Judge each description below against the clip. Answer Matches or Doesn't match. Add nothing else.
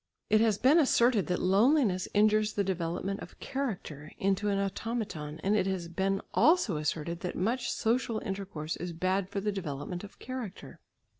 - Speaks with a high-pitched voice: Matches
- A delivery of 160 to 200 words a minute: Matches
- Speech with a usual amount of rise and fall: Matches